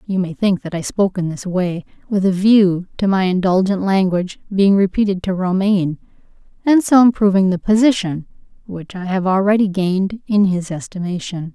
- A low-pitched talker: No, high, 190 Hz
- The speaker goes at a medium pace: Yes, average, 170 wpm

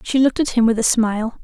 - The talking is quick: Yes, fast, 295 wpm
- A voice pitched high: Yes, high, 235 Hz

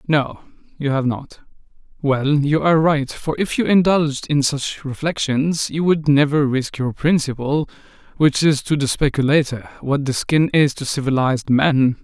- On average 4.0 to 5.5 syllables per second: Yes, 4.6 syllables/s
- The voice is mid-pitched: Yes, medium, 145 Hz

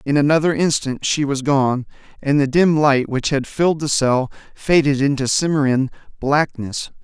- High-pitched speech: No, medium, 140 Hz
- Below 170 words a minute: Yes, average, 160 wpm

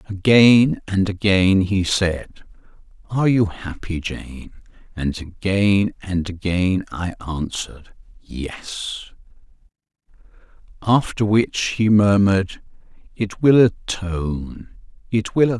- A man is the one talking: Yes, male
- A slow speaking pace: Yes, slow, 95 wpm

